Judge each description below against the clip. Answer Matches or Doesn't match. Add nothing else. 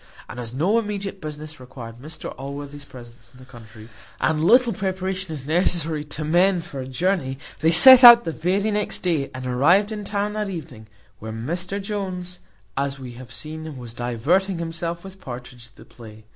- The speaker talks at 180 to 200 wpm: Matches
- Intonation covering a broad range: Matches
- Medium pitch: Matches